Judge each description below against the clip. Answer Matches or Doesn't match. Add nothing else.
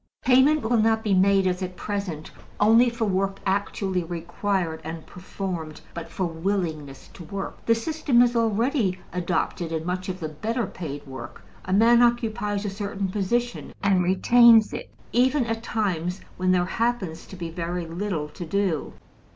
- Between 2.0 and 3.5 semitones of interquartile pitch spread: Doesn't match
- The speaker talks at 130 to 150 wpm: Doesn't match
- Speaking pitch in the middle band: Doesn't match